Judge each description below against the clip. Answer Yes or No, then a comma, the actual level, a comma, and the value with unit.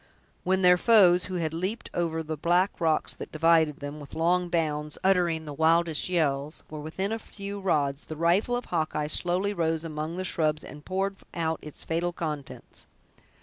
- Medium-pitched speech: Yes, medium, 165 Hz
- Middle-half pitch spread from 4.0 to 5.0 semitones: No, average, 2.7 semitones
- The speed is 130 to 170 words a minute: No, average, 180 wpm